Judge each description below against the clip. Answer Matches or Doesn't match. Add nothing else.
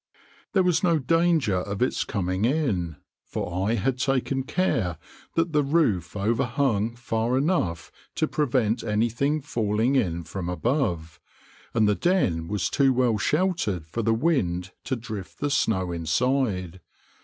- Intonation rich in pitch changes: Matches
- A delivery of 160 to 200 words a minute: Doesn't match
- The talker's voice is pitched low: Matches